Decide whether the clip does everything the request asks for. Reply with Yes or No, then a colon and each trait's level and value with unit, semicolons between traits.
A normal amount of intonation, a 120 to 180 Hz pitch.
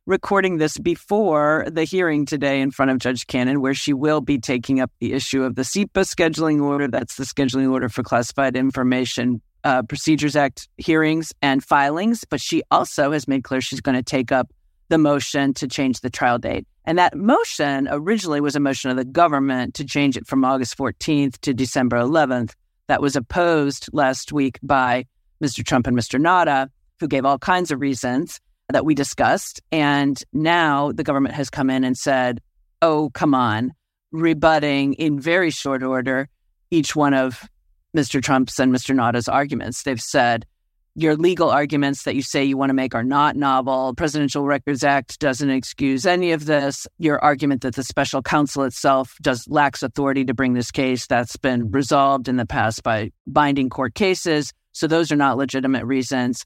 No: narrow, 2.3 semitones; medium, 140 Hz